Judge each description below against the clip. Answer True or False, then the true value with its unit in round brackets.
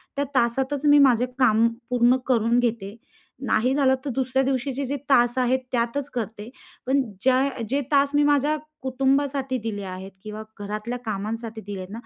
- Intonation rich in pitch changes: False (3.3 semitones)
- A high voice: True (250 Hz)